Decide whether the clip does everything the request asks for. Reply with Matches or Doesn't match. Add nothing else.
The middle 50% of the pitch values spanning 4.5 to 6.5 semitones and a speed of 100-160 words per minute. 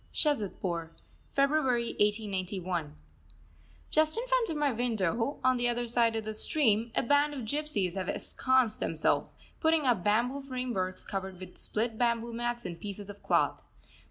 Matches